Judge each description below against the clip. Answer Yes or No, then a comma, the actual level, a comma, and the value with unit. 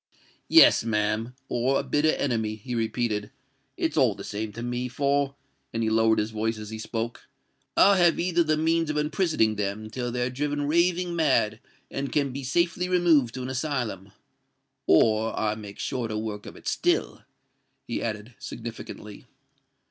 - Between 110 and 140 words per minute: No, average, 150 wpm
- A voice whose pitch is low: Yes, low, 120 Hz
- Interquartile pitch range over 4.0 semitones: Yes, average, 5.1 semitones